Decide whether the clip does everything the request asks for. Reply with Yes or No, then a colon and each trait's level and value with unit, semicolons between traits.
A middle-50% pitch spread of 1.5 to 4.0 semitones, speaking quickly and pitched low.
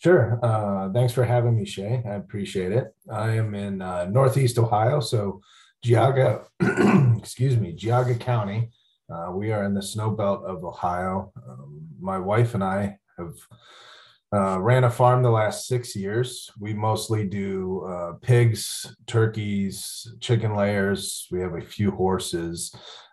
No: average, 3.7 semitones; average, 150 wpm; low, 110 Hz